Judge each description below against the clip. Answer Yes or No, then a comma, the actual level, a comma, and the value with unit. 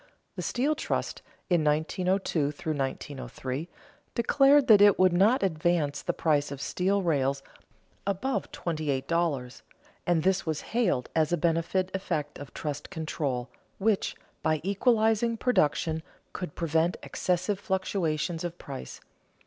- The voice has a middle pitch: Yes, medium, 170 Hz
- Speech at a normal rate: No, slow, 130 wpm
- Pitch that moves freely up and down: No, average, 4.5 semitones